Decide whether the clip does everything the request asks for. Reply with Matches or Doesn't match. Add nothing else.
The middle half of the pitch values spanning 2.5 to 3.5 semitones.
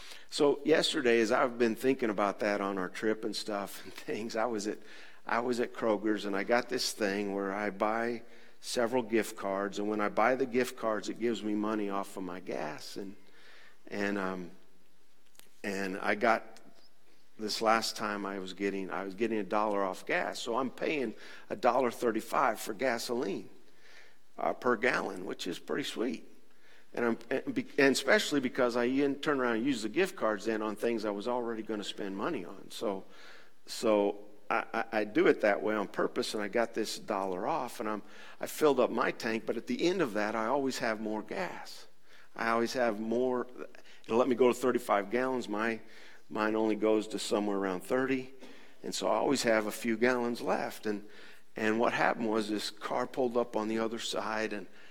Matches